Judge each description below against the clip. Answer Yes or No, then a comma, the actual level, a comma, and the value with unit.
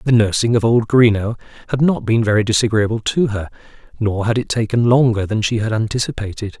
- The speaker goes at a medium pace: Yes, average, 190 wpm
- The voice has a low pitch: Yes, low, 110 Hz